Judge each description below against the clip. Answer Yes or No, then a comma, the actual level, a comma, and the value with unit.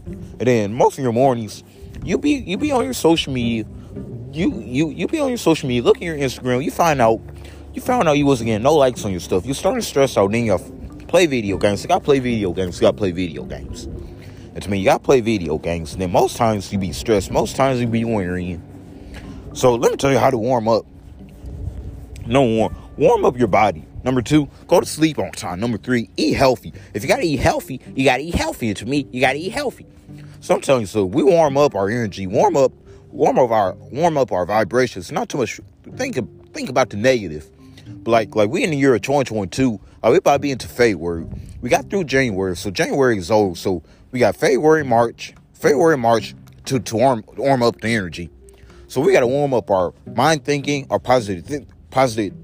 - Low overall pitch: Yes, low, 115 Hz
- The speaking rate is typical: No, fast, 230 wpm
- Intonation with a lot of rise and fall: Yes, wide, 6.1 semitones